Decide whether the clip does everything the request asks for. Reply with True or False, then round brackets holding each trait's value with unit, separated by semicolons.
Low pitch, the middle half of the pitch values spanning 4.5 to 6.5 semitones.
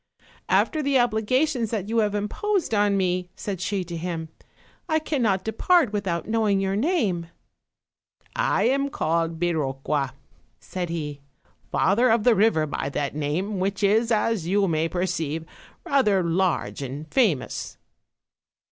False (195 Hz; 5.2 semitones)